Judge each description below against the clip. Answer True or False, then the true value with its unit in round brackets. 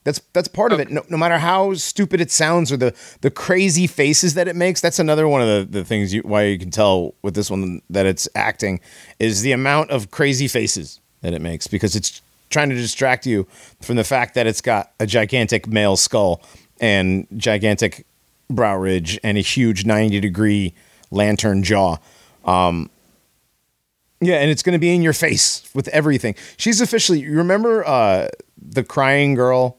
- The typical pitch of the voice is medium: False (120 Hz)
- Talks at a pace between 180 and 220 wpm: True (185 wpm)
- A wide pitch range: True (7.1 semitones)